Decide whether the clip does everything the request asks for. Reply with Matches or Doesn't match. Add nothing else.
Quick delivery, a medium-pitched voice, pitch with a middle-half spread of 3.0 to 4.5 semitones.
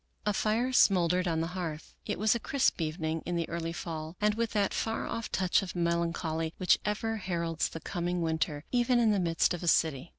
Matches